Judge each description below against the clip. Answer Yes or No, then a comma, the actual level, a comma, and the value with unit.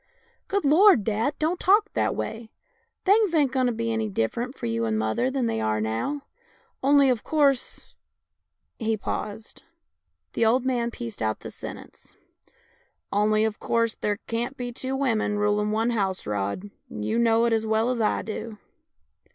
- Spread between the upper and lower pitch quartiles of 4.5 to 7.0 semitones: No, average, 4.0 semitones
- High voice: Yes, high, 230 Hz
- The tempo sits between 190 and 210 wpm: No, average, 180 wpm